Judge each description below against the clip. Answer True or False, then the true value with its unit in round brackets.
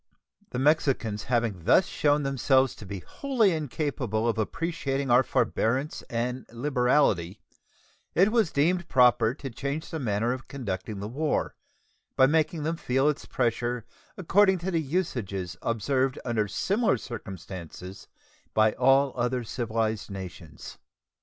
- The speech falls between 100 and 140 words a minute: True (135 wpm)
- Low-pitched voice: True (125 Hz)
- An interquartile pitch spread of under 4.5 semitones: False (5.2 semitones)